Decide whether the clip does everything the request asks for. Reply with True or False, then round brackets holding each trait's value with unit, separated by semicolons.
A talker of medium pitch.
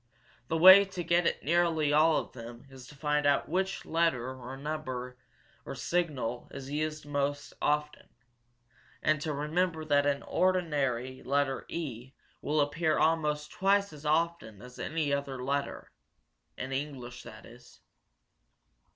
True (150 Hz)